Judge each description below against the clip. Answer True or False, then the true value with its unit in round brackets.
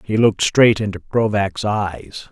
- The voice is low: True (105 Hz)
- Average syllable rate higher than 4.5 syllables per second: False (4.2 syllables/s)